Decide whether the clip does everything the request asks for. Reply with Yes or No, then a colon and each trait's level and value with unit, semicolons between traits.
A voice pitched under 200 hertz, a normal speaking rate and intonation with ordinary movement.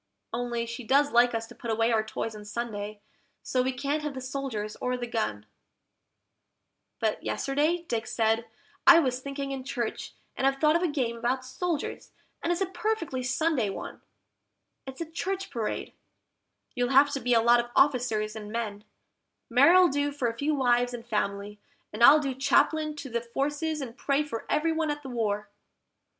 No: very high, 255 Hz; average, 185 wpm; average, 4.0 semitones